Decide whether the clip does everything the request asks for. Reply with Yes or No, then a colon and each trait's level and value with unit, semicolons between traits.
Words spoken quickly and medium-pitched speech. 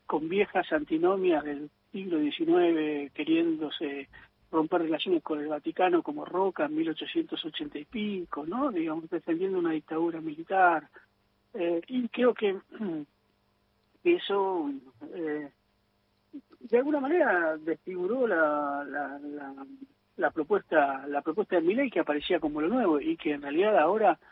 No: average, 135 wpm; medium, 175 Hz